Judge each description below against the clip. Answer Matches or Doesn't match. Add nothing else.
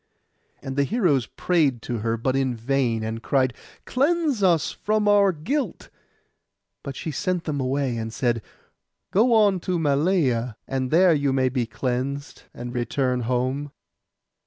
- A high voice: Doesn't match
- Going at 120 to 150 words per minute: Matches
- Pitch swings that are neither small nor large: Doesn't match